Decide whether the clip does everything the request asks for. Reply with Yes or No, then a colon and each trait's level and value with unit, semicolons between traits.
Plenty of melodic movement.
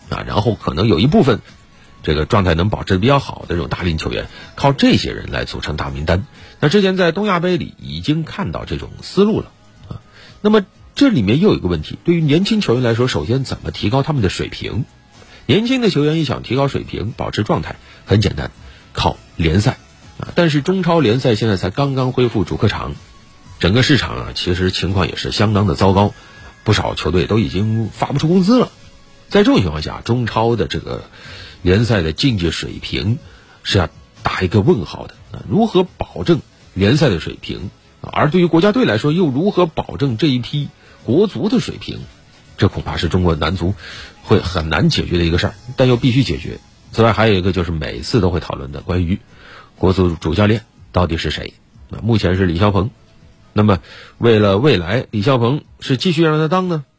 Yes: wide, 7.2 semitones